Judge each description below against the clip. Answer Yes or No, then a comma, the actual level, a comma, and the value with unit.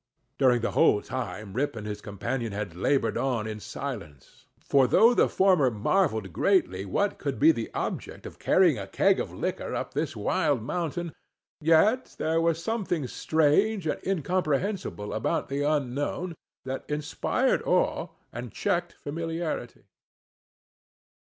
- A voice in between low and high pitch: Yes, medium, 145 Hz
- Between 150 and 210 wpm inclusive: No, average, 140 wpm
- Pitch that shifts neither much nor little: No, wide, 7.1 semitones